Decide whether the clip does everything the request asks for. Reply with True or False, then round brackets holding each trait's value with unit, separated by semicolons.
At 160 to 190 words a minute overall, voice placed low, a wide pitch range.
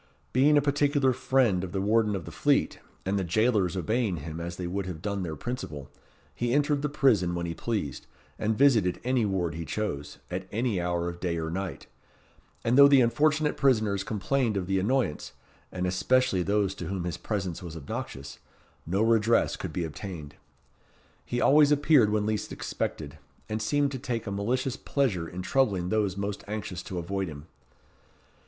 True (180 wpm; 100 Hz; 5.9 semitones)